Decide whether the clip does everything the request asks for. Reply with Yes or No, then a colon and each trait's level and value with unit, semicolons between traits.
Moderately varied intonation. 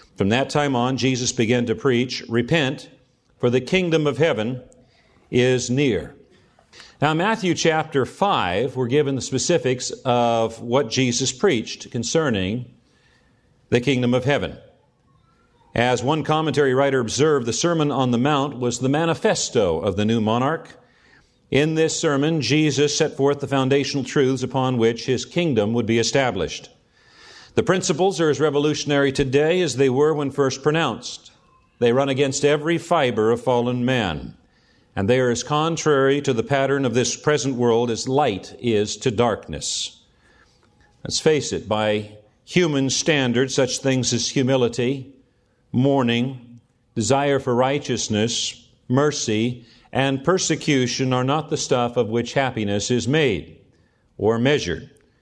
Yes: average, 3.3 semitones